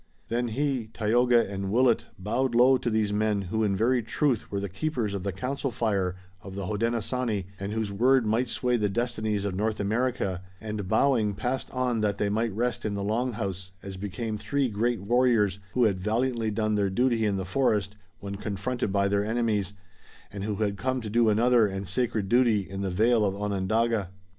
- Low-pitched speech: Yes, low, 110 Hz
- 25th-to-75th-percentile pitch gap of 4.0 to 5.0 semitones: No, average, 3.3 semitones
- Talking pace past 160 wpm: Yes, average, 195 wpm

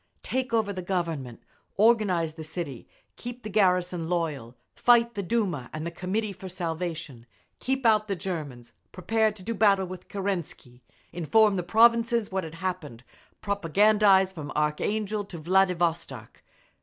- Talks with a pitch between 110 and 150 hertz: No, medium, 185 Hz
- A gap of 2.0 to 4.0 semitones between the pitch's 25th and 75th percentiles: No, average, 4.6 semitones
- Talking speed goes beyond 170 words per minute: No, average, 145 wpm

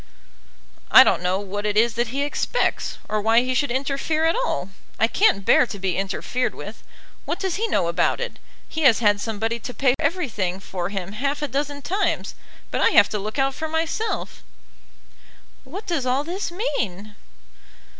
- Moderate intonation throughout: No, wide, 7.0 semitones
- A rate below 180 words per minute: No, average, 185 wpm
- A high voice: Yes, very high, 250 Hz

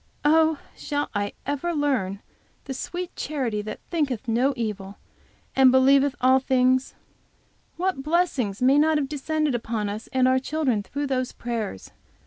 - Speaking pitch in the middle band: No, very high, 265 Hz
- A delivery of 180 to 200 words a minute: No, average, 145 wpm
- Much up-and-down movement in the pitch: No, average, 4.0 semitones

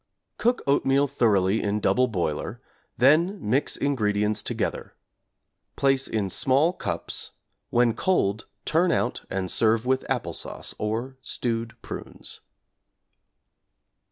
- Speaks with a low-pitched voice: Yes, low, 120 Hz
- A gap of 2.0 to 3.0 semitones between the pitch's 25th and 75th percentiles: No, average, 4.6 semitones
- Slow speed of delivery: Yes, slow, 110 wpm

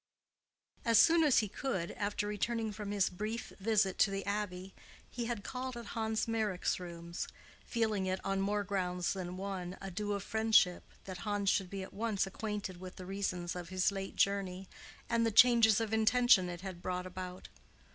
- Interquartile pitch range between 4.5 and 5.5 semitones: No, average, 3.0 semitones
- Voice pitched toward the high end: Yes, high, 200 Hz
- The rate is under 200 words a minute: Yes, average, 185 wpm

